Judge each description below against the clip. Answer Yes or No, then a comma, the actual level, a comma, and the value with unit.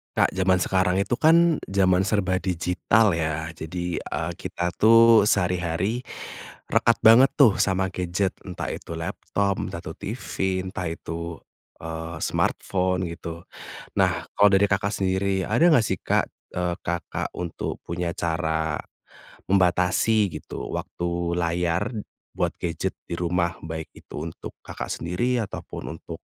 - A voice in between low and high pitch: No, very low, 90 Hz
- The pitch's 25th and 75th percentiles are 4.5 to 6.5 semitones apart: No, average, 2.8 semitones